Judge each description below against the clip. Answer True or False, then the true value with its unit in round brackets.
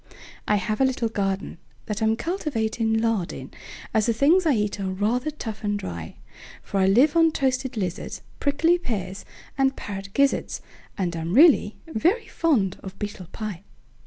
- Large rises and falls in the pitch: True (6.0 semitones)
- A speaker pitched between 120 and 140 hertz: False (220 Hz)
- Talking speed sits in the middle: True (145 wpm)